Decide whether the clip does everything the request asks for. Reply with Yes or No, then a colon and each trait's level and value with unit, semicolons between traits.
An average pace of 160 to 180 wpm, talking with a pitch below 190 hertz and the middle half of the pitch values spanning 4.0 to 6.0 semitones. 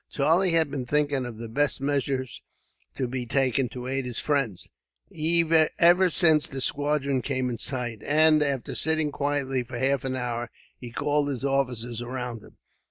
No: average, 165 wpm; low, 135 Hz; average, 3.0 semitones